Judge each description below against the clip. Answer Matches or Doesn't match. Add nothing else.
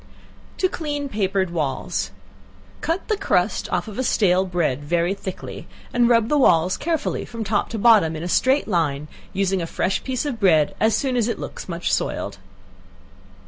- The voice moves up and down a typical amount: Doesn't match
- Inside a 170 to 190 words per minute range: Matches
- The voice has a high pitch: Matches